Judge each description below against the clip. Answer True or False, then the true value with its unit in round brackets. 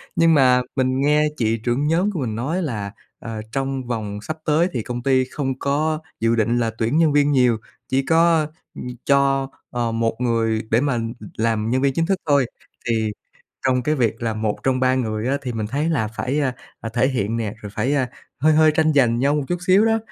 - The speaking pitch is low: True (130 Hz)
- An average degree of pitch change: True (4.3 semitones)